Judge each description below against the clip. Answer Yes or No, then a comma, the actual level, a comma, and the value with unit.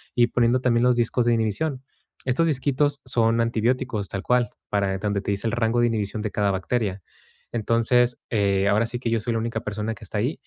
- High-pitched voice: No, low, 115 Hz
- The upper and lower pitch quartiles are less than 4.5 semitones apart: Yes, average, 2.7 semitones